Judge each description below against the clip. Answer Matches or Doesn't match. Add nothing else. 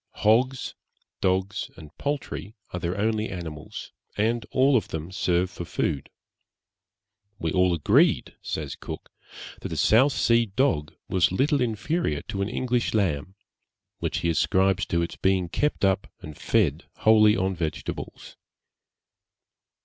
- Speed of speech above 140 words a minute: Doesn't match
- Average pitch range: Matches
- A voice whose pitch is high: Doesn't match